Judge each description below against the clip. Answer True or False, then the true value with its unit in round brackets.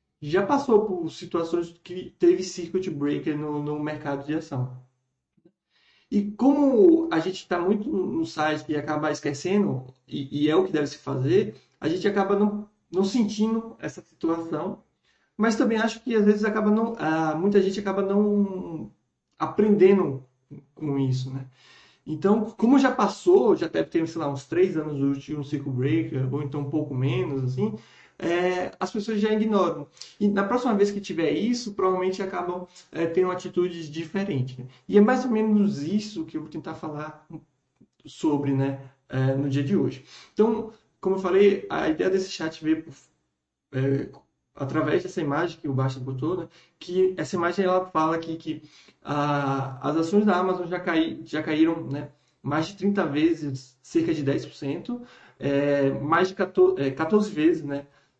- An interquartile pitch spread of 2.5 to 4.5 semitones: False (5.4 semitones)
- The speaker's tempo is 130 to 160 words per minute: False (170 wpm)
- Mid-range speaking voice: True (165 Hz)